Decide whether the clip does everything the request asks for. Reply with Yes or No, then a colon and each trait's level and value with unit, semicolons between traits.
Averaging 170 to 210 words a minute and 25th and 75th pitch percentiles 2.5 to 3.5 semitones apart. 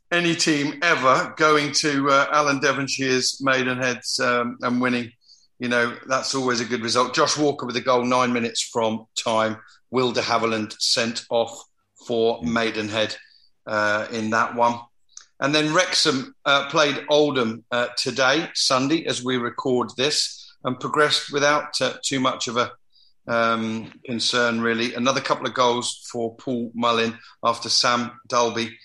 No: average, 150 wpm; average, 2.9 semitones